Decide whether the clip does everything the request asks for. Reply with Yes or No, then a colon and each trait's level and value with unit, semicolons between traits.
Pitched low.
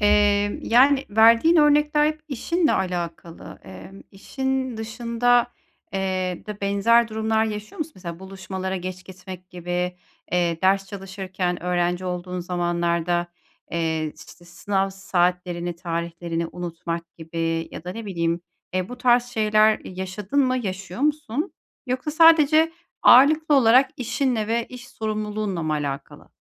No: high, 195 Hz